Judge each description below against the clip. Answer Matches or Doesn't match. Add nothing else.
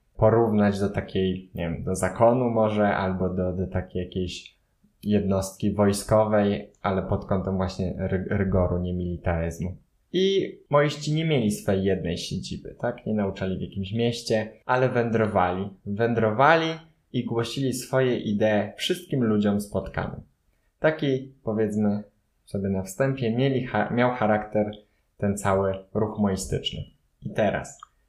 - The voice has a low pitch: Matches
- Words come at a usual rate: Matches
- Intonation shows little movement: Doesn't match